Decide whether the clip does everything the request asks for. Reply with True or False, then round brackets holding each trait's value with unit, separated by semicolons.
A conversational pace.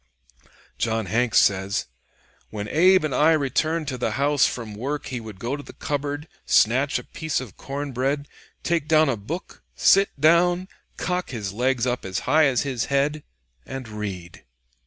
True (170 wpm)